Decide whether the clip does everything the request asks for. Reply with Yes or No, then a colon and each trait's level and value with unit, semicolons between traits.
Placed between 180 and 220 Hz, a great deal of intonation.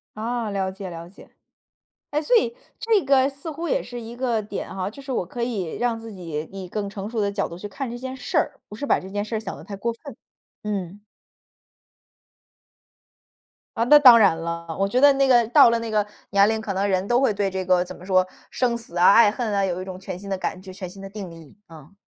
No: high, 205 Hz; average, 4.3 semitones